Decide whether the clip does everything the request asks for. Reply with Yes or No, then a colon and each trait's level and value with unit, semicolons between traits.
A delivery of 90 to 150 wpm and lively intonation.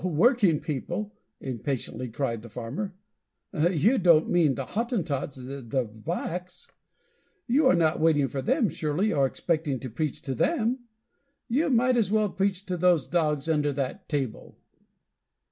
Yes: average, 145 wpm; wide, 6.6 semitones